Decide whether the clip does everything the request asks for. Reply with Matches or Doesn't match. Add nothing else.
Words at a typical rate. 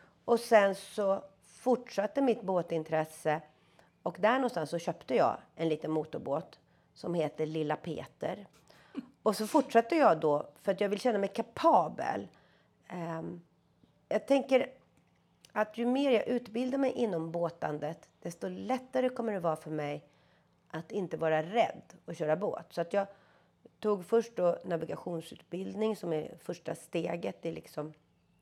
Matches